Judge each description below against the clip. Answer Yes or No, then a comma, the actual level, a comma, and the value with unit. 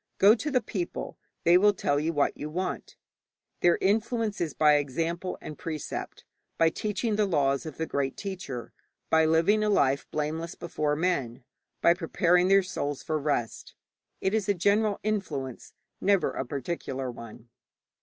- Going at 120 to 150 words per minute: No, average, 160 wpm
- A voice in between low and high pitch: Yes, medium, 165 Hz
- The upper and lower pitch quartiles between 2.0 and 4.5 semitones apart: No, wide, 5.5 semitones